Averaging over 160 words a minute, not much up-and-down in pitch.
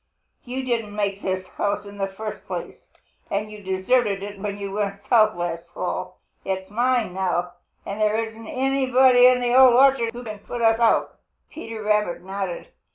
No: average, 175 wpm; average, 3.5 semitones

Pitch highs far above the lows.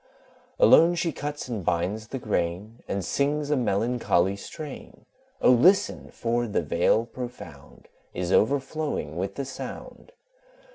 Yes: wide, 6.7 semitones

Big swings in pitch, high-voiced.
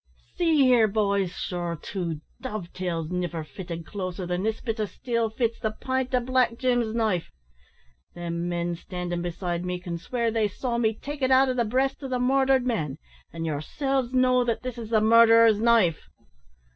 Yes: wide, 6.0 semitones; high, 220 Hz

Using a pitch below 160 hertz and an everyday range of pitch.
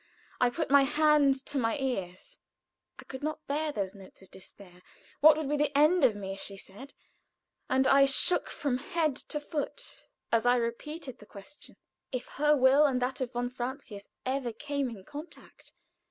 No: very high, 270 Hz; average, 3.9 semitones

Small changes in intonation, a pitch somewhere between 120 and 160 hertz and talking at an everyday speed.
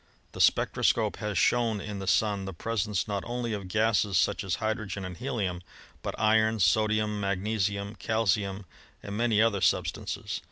No: narrow, 2.1 semitones; low, 105 Hz; average, 165 wpm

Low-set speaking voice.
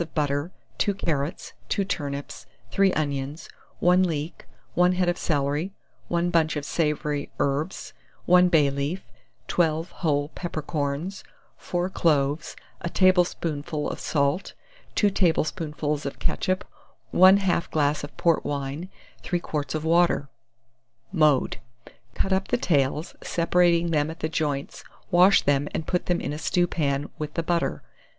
No: medium, 160 Hz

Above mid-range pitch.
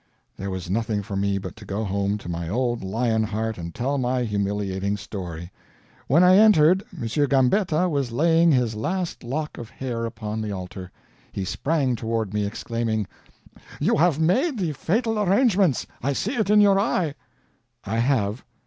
No: low, 120 Hz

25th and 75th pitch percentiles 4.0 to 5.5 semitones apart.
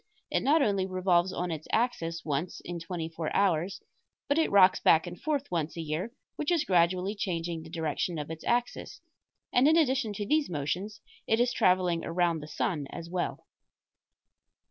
Yes: average, 4.6 semitones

